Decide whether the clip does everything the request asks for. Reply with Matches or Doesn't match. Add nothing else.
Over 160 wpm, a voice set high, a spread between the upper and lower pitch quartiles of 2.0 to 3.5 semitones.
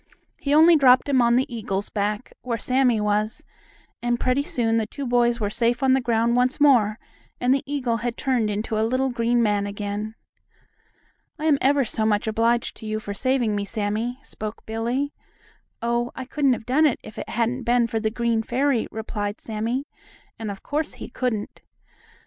Matches